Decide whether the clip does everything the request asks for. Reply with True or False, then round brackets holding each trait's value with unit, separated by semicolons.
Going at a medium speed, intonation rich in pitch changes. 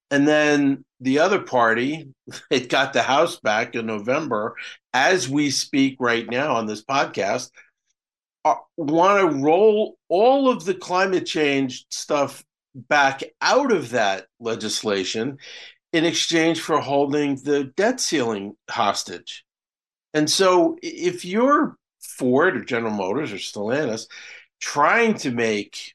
False (125 wpm; 6.7 semitones)